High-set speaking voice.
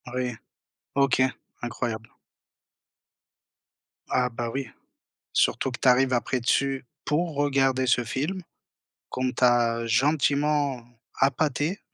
No: low, 130 Hz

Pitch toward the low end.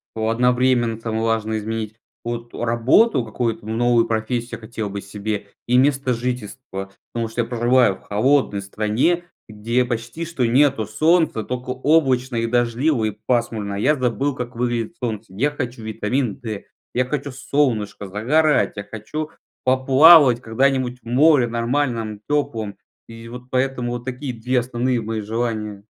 Yes: low, 120 Hz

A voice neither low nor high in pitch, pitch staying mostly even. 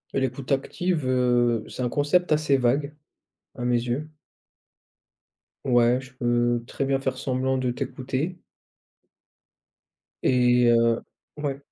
No: low, 130 Hz; narrow, 2.2 semitones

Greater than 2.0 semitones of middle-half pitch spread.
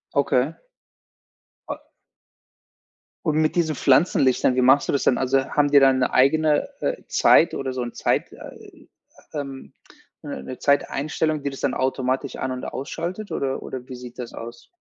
Yes: narrow, 2.5 semitones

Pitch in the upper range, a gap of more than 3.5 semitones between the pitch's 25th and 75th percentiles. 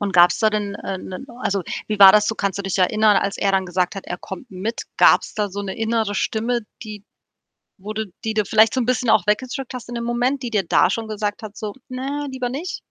No: high, 215 Hz; average, 3.1 semitones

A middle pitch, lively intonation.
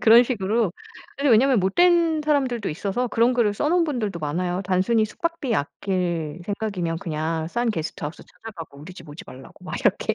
No: high, 205 Hz; wide, 6.3 semitones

